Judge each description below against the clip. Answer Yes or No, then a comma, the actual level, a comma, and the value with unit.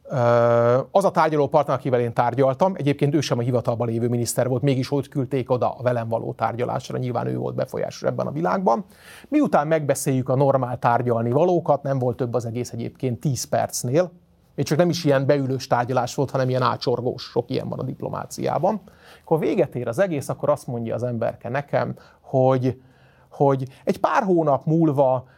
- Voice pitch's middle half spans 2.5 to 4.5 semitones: Yes, average, 2.9 semitones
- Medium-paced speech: No, fast, 180 wpm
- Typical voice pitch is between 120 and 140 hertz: Yes, low, 130 Hz